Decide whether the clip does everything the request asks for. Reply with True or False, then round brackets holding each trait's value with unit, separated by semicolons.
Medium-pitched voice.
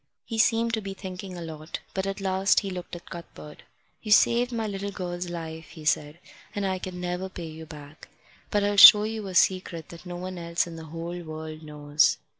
True (180 Hz)